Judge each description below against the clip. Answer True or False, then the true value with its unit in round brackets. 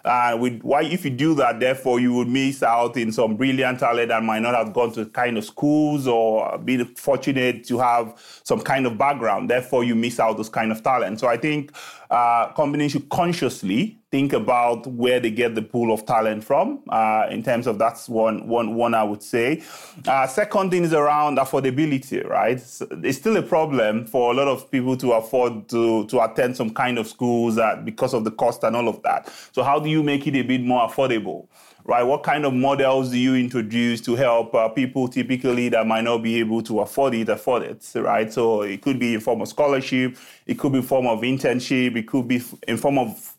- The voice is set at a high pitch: False (125 Hz)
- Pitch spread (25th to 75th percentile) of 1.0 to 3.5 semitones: True (2.8 semitones)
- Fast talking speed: True (220 wpm)